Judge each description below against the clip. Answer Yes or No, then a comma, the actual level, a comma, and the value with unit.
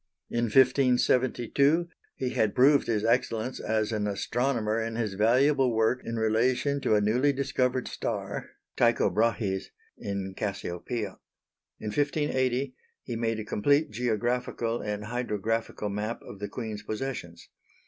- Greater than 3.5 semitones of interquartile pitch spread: No, average, 3.2 semitones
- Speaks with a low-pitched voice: Yes, low, 115 Hz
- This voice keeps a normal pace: No, slow, 130 wpm